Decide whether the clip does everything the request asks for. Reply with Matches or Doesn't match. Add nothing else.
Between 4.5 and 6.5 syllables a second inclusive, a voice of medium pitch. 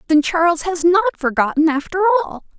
Doesn't match